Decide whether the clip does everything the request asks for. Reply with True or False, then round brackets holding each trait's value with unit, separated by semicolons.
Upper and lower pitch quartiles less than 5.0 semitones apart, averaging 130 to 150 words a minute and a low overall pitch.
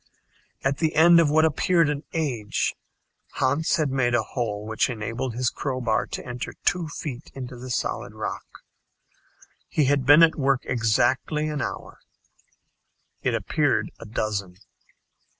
True (4.1 semitones; 145 wpm; 130 Hz)